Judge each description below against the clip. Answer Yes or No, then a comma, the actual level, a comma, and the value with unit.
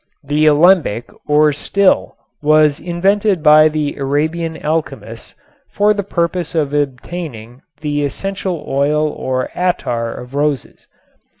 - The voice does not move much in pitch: No, average, 3.2 semitones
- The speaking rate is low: Yes, slow, 115 wpm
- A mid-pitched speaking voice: Yes, medium, 150 Hz